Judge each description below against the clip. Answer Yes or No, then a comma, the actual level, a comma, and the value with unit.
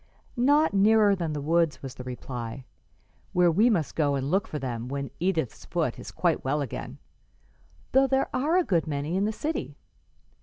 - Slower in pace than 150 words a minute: No, average, 185 wpm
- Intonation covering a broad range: Yes, wide, 7.0 semitones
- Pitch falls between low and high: Yes, medium, 165 Hz